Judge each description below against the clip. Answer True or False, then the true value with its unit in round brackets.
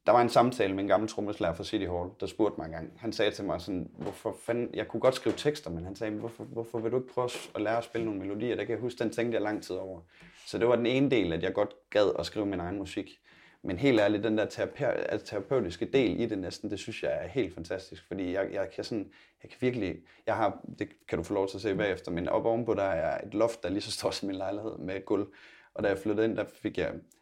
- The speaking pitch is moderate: False (110 Hz)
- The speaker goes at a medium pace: False (280 wpm)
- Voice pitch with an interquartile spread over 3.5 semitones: False (3.1 semitones)